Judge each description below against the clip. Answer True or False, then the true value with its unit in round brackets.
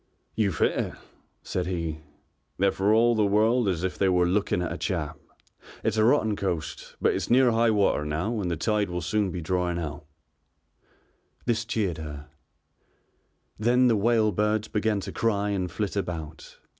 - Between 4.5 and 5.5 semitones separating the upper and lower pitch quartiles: False (3.9 semitones)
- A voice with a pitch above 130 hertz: False (100 Hz)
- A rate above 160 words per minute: True (175 wpm)